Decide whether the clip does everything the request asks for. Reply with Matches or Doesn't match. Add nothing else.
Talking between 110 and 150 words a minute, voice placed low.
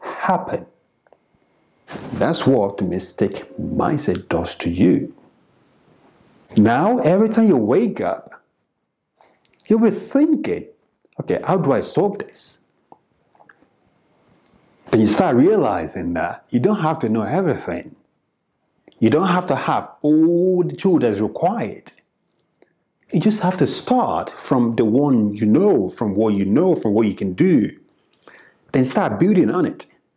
Doesn't match